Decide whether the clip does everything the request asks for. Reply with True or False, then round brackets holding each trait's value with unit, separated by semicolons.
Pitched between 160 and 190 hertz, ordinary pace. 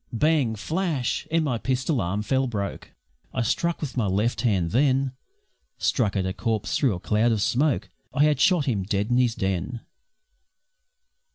False (120 Hz; 170 wpm)